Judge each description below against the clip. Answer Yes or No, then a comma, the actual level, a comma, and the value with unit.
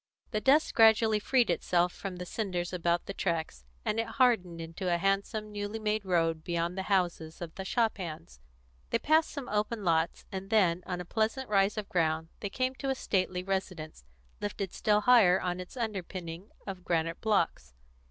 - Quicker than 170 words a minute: Yes, average, 180 wpm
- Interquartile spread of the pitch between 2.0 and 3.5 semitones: No, average, 3.9 semitones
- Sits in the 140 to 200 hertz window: Yes, high, 190 Hz